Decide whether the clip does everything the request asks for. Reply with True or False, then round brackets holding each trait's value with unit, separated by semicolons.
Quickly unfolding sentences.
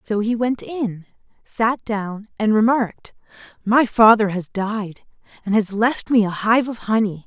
False (165 wpm)